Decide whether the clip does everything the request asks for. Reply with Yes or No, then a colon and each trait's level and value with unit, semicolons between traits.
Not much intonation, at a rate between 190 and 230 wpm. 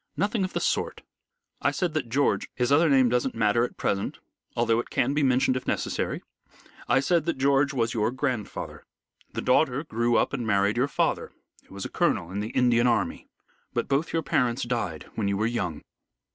No: average, 3.5 semitones; average, 200 wpm